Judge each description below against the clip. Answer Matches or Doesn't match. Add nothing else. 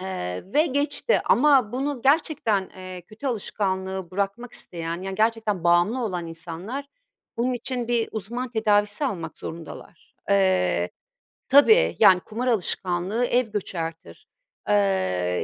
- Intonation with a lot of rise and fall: Matches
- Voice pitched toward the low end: Doesn't match